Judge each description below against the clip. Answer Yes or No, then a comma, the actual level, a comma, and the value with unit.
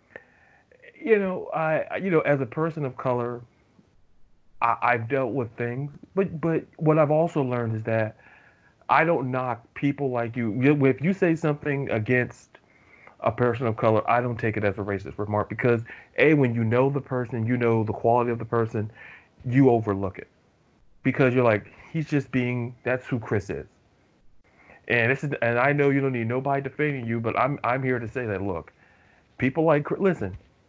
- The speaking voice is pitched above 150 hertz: No, low, 125 Hz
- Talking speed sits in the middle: Yes, average, 190 wpm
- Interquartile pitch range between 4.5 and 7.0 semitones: No, average, 3.8 semitones